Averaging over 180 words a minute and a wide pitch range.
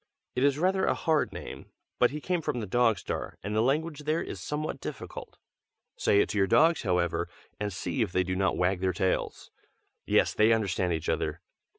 Yes: fast, 205 wpm; wide, 8.0 semitones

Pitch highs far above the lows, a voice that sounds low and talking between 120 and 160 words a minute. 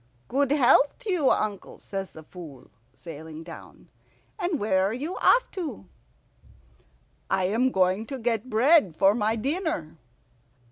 No: wide, 7.4 semitones; high, 220 Hz; average, 140 wpm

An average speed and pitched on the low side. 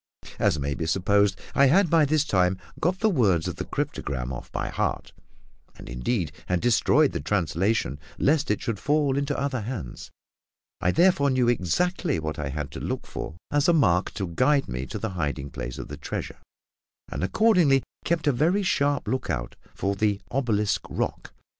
Yes: average, 180 wpm; low, 105 Hz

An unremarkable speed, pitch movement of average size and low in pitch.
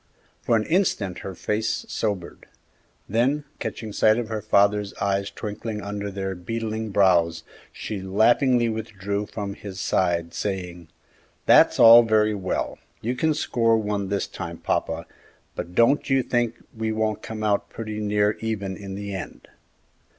No: average, 150 wpm; narrow, 2.3 semitones; low, 105 Hz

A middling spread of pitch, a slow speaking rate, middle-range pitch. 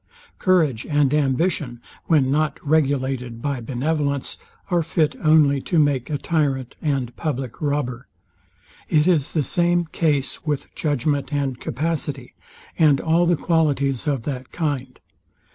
Yes: average, 3.0 semitones; slow, 130 wpm; medium, 145 Hz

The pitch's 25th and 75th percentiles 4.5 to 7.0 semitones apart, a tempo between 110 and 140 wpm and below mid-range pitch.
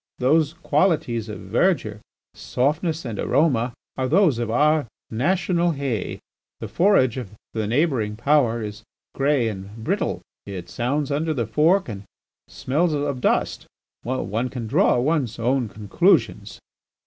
Yes: average, 5.2 semitones; slow, 135 wpm; low, 130 Hz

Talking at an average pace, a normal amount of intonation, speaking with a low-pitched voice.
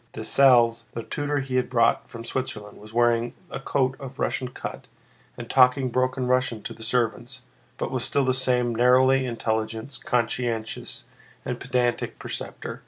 No: average, 155 wpm; narrow, 2.0 semitones; low, 125 Hz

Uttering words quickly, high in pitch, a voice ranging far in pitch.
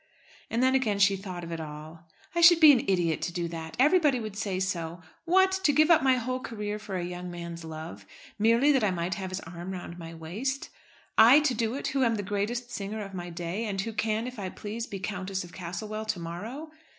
Yes: fast, 235 wpm; high, 200 Hz; wide, 5.7 semitones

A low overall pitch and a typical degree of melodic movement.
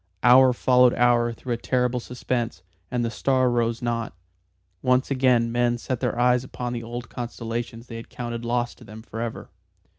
No: low, 120 Hz; narrow, 1.2 semitones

